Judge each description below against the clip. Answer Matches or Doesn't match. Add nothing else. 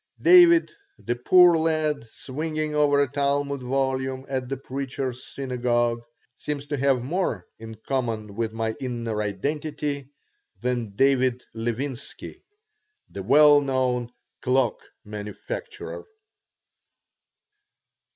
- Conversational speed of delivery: Doesn't match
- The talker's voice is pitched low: Matches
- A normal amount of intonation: Matches